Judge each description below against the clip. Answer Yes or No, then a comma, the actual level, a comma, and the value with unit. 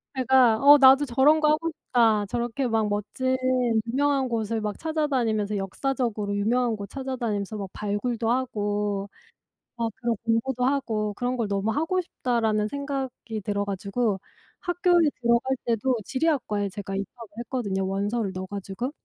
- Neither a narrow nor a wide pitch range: Yes, average, 4.2 semitones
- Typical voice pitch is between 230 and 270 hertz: Yes, high, 235 Hz